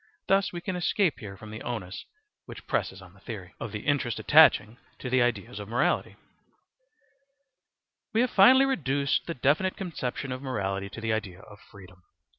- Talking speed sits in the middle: Yes, average, 175 wpm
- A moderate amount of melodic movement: No, wide, 8.6 semitones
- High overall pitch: No, low, 125 Hz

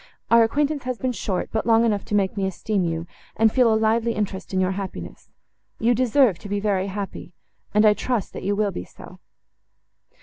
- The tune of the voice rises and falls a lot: No, average, 3.1 semitones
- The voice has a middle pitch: No, high, 210 Hz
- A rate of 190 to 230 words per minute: Yes, fast, 205 wpm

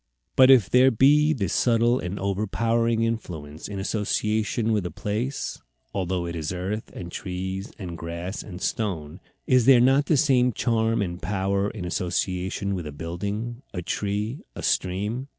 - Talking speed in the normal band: Yes, average, 165 wpm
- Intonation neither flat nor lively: Yes, average, 4.3 semitones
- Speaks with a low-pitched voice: Yes, low, 100 Hz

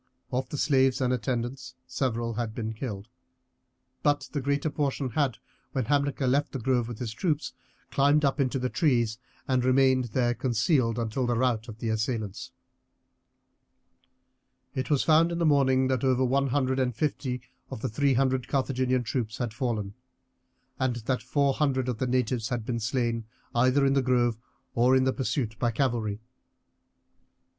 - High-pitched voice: No, low, 130 Hz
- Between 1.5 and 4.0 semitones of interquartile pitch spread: Yes, narrow, 2.5 semitones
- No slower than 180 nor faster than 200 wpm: No, average, 165 wpm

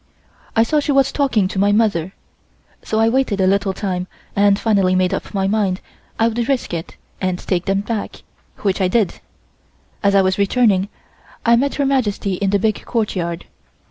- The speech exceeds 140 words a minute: Yes, average, 185 wpm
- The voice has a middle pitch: No, high, 200 Hz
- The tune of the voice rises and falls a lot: No, average, 3.3 semitones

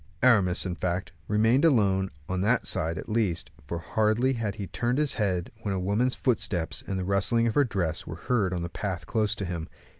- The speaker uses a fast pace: Yes, fast, 210 wpm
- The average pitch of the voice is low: Yes, low, 100 Hz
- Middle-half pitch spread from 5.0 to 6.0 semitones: No, average, 4.1 semitones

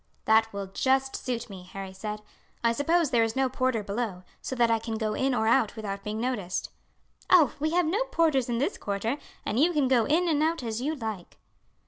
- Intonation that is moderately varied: Yes, average, 4.7 semitones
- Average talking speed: No, fast, 215 wpm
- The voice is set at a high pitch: Yes, high, 235 Hz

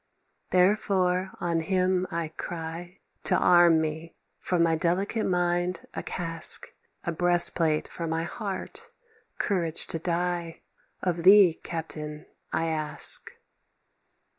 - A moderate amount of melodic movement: No, narrow, 1.9 semitones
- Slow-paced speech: Yes, slow, 115 wpm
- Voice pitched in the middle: Yes, medium, 175 Hz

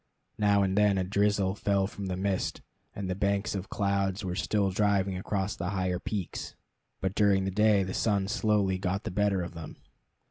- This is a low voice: Yes, low, 100 Hz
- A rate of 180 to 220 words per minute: Yes, average, 190 wpm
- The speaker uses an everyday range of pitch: No, narrow, 1.4 semitones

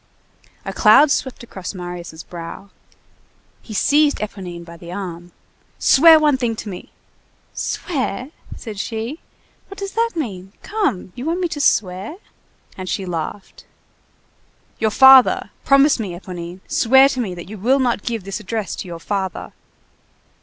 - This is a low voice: No, high, 215 Hz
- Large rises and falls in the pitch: Yes, wide, 6.7 semitones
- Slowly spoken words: No, average, 150 wpm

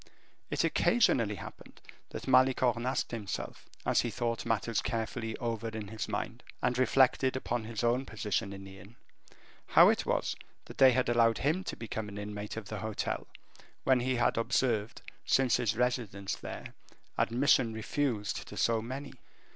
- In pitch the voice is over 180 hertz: No, low, 115 Hz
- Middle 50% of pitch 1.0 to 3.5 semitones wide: Yes, average, 2.9 semitones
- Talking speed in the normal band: Yes, average, 165 wpm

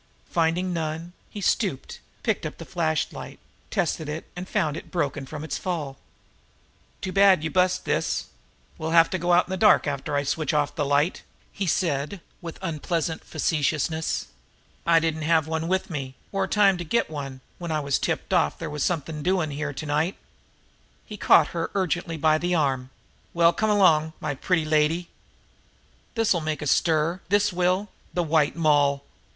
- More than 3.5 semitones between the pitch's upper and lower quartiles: No, average, 3.0 semitones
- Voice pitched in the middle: Yes, medium, 160 Hz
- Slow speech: No, average, 175 wpm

